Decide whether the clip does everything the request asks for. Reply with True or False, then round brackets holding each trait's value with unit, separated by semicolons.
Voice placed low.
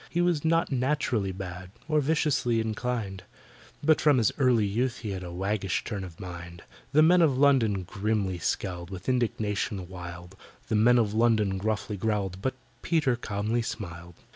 True (110 Hz)